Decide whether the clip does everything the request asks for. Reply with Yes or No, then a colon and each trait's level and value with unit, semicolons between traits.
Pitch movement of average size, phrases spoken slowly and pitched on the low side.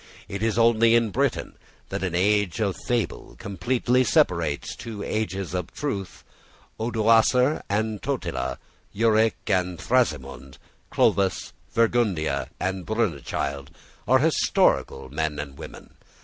Yes: average, 4.8 semitones; slow, 115 wpm; low, 105 Hz